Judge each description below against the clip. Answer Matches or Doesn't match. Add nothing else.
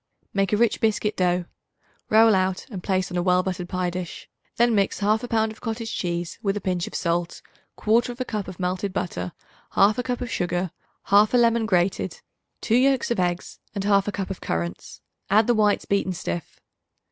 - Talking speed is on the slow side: Doesn't match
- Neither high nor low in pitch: Doesn't match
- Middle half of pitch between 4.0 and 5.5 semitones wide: Doesn't match